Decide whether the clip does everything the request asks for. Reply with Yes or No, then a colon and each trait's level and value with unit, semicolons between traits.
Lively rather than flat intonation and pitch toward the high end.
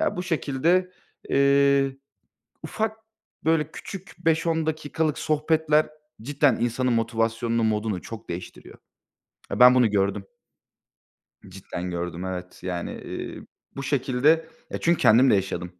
No: wide, 6.5 semitones; low, 130 Hz